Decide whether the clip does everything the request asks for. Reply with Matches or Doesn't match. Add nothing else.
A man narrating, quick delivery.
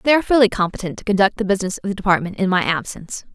Doesn't match